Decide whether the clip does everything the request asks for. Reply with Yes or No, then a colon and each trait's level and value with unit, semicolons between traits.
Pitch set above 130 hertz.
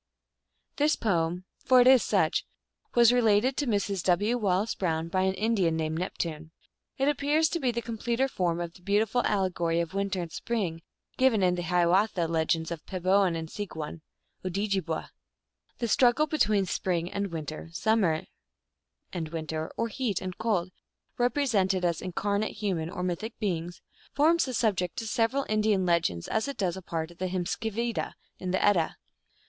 Yes: high, 190 Hz